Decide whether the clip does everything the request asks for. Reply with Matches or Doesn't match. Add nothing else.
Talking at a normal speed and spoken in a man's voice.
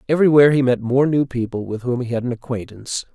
Doesn't match